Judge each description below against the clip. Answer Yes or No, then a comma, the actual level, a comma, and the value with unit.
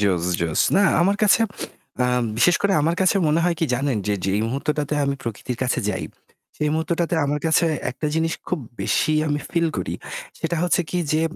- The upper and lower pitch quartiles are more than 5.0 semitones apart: Yes, wide, 5.4 semitones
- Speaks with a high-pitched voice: No, medium, 150 Hz